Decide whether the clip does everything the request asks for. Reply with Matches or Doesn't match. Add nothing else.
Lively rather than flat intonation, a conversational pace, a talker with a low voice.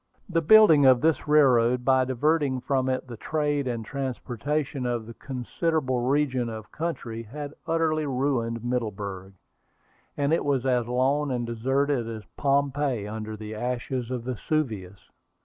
Doesn't match